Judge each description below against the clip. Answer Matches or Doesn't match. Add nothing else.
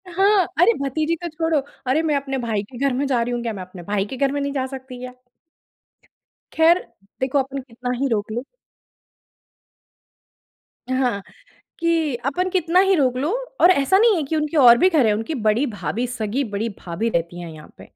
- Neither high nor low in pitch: Doesn't match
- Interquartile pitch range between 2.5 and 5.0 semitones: Doesn't match